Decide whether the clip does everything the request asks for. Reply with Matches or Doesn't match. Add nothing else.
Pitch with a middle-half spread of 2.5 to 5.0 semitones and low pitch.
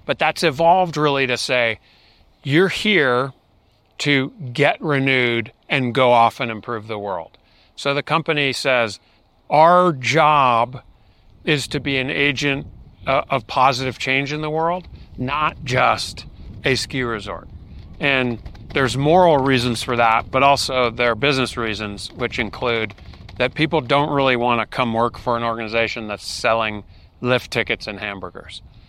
Matches